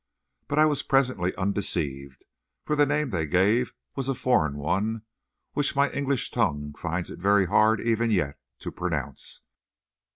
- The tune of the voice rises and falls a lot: Yes, wide, 7.5 semitones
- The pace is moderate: Yes, average, 155 wpm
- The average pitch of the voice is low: Yes, low, 105 Hz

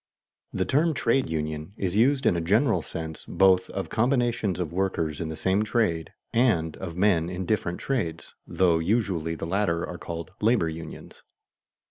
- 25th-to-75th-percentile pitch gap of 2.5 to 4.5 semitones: No, average, 4.9 semitones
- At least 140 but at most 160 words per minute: No, average, 170 wpm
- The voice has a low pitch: Yes, very low, 90 Hz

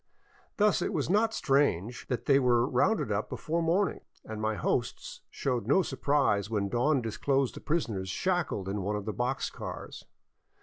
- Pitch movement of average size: No, wide, 6.7 semitones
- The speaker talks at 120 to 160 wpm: No, average, 170 wpm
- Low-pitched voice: Yes, low, 125 Hz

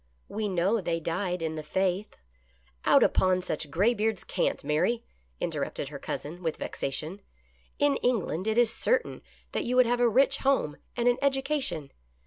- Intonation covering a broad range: Yes, wide, 7.0 semitones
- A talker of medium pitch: No, high, 195 Hz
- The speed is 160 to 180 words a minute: Yes, average, 175 wpm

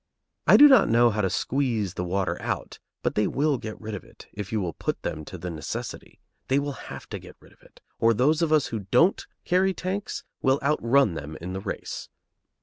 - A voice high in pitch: No, low, 115 Hz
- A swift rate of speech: Yes, fast, 225 wpm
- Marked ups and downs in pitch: Yes, wide, 7.0 semitones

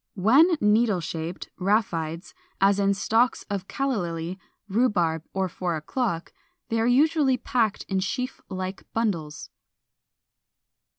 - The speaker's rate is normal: No, slow, 120 wpm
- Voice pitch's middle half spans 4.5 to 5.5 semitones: Yes, average, 5.1 semitones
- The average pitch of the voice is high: Yes, high, 200 Hz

